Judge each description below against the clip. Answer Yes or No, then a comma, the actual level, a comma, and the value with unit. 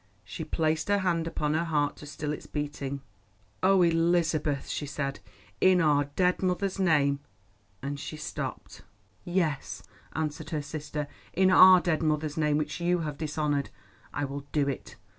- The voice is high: No, medium, 155 Hz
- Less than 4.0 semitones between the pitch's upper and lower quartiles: Yes, average, 2.8 semitones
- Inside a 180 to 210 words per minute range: No, average, 160 wpm